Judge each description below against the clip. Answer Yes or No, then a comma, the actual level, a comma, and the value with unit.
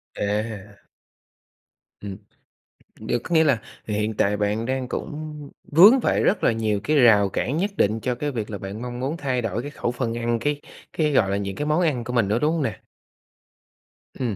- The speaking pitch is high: No, low, 120 Hz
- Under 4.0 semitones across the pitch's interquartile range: No, wide, 5.6 semitones